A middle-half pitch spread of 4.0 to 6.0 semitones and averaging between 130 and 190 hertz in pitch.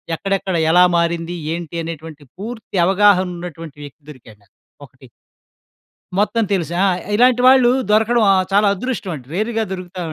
Yes: average, 4.4 semitones; medium, 185 Hz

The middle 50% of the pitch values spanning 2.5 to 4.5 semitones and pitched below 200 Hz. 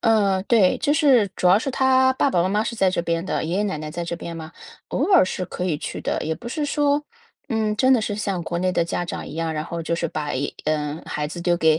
No: wide, 5.6 semitones; medium, 185 Hz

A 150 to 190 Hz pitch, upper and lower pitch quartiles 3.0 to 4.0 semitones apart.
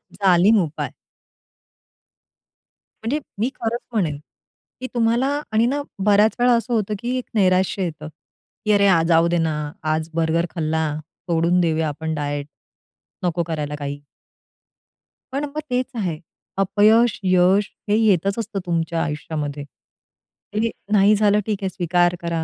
No: medium, 185 Hz; average, 4.9 semitones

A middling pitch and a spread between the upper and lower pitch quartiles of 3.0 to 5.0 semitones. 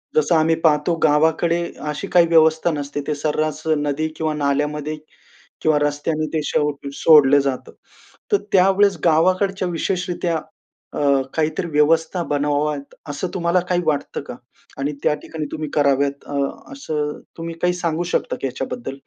No: medium, 155 Hz; narrow, 2.4 semitones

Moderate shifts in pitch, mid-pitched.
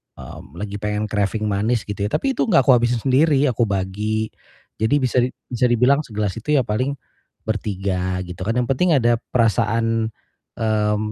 No: average, 3.1 semitones; low, 110 Hz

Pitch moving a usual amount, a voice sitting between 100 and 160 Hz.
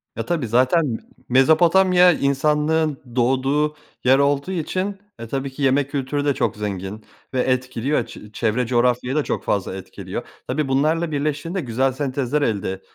Yes: average, 3.4 semitones; low, 135 Hz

